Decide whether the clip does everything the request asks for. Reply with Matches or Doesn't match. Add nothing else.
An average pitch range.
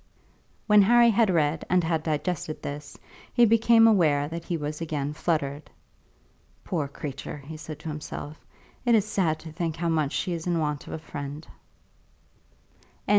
Matches